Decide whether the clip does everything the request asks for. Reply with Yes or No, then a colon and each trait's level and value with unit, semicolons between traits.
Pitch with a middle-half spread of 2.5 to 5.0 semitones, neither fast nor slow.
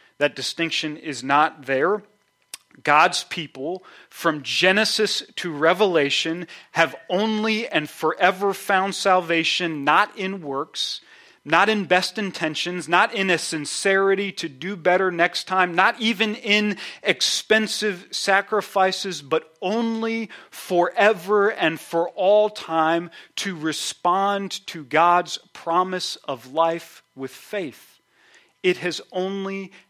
No: average, 3.5 semitones; slow, 115 wpm